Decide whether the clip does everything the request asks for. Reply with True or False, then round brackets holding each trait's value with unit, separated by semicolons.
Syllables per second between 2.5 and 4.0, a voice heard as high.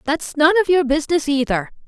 False (6.0 syllables/s; 295 Hz)